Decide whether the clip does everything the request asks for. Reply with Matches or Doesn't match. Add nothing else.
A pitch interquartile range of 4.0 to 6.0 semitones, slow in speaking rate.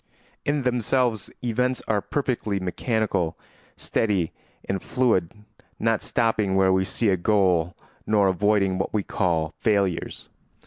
Doesn't match